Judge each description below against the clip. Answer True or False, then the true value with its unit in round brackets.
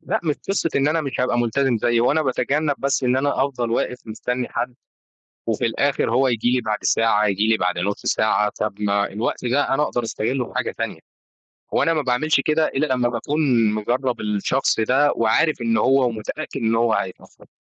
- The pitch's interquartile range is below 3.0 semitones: False (3.6 semitones)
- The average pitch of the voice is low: True (125 Hz)